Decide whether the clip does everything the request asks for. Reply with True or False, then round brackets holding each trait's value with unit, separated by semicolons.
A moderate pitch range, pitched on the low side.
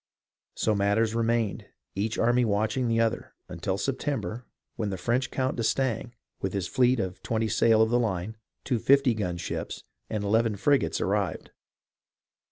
True (3.1 semitones; 115 Hz)